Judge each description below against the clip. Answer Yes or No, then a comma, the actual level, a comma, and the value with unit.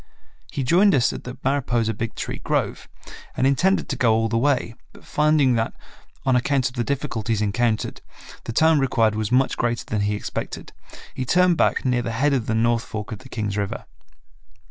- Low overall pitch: Yes, low, 120 Hz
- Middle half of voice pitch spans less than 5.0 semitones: Yes, average, 3.5 semitones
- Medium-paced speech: Yes, average, 195 wpm